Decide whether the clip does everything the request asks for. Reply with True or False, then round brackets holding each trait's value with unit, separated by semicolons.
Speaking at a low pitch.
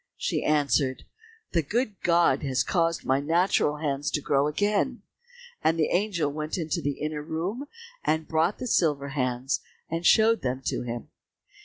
False (155 Hz)